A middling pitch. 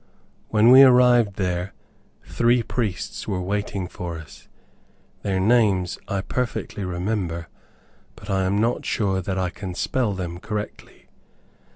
No: low, 100 Hz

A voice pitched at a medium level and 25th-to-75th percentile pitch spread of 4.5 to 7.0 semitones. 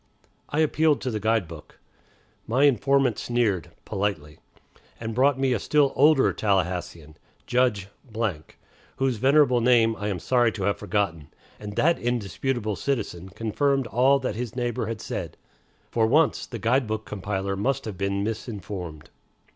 No: low, 115 Hz; average, 4.8 semitones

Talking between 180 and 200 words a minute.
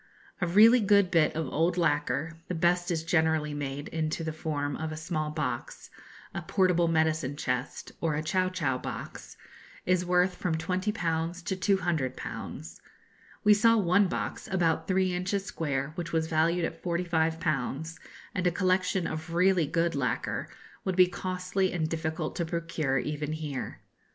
No: average, 155 wpm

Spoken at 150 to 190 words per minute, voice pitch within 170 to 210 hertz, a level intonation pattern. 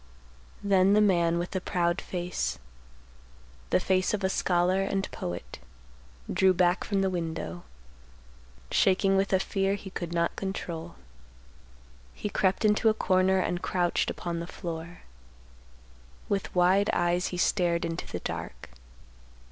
No: average, 140 wpm; medium, 185 Hz; narrow, 1.9 semitones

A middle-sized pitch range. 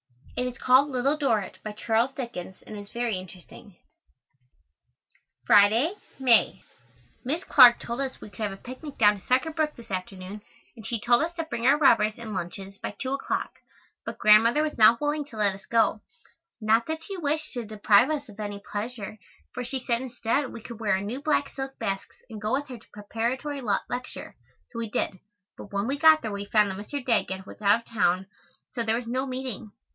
Yes: average, 4.3 semitones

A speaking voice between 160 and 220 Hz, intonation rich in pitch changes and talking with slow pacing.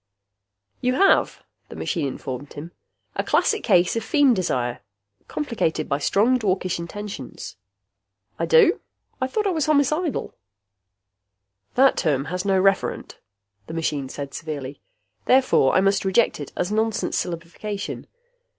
Yes: high, 190 Hz; wide, 8.0 semitones; slow, 130 wpm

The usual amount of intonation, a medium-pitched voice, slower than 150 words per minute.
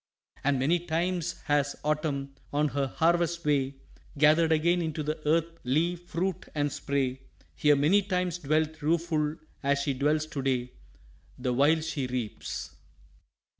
Yes: average, 3.1 semitones; medium, 155 Hz; average, 140 wpm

